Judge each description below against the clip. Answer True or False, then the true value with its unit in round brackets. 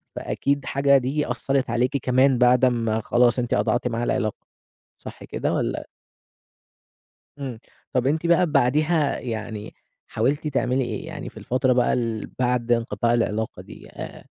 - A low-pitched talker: True (125 Hz)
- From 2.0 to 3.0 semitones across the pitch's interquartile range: True (2.7 semitones)